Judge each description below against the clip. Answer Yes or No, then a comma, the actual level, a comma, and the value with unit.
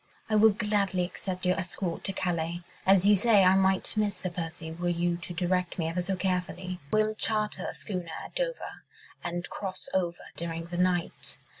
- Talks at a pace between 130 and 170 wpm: No, average, 185 wpm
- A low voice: No, medium, 185 Hz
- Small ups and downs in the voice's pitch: Yes, narrow, 2.2 semitones